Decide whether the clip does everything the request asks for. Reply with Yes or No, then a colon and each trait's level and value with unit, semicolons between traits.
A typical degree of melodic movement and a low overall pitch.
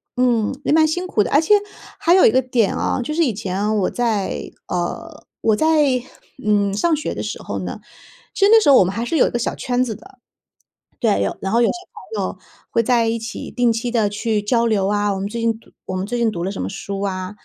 No: average, 3.7 semitones; high, 230 Hz